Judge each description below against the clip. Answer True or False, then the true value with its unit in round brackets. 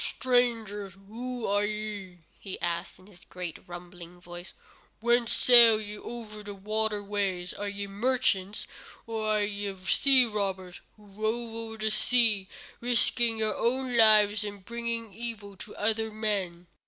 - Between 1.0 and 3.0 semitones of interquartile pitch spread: True (2.5 semitones)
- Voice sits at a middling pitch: False (210 Hz)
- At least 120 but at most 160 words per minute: True (145 wpm)